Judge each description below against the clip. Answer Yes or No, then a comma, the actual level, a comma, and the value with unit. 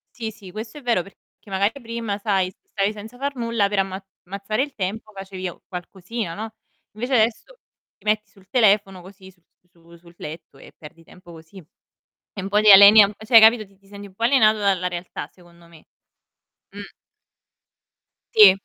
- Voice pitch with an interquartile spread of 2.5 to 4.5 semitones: Yes, average, 2.9 semitones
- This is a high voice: Yes, high, 200 Hz